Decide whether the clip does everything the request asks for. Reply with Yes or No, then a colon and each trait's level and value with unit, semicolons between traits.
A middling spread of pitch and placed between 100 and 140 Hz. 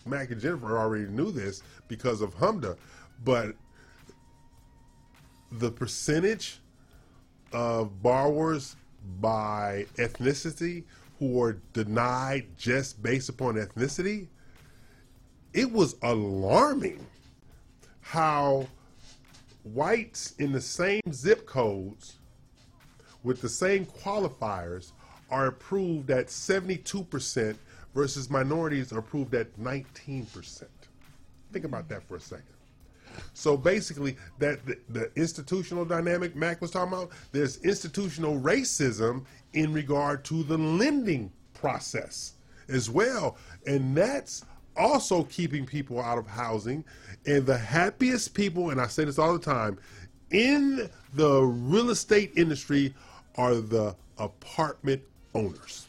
No: wide, 5.7 semitones; low, 135 Hz